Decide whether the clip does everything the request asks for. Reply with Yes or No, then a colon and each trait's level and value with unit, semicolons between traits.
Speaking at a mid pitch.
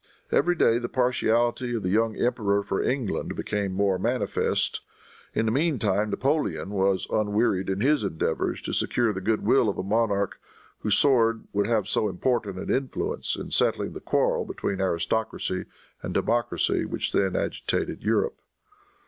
No: low, 110 Hz